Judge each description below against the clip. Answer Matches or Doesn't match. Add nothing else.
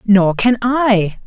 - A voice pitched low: Doesn't match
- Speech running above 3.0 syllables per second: Doesn't match